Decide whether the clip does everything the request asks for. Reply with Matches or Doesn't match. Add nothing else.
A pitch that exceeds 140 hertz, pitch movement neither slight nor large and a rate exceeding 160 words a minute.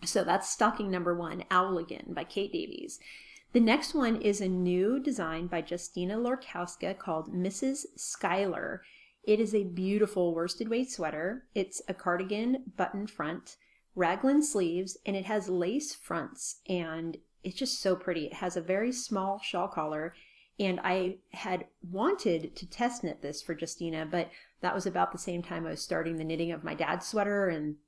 Matches